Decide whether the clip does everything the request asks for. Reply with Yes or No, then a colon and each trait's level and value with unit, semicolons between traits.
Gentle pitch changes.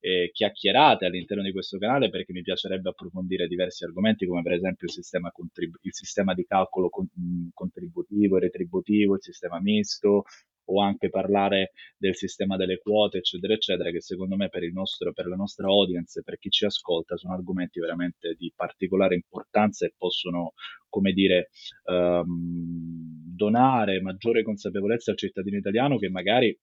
Yes: narrow, 2.2 semitones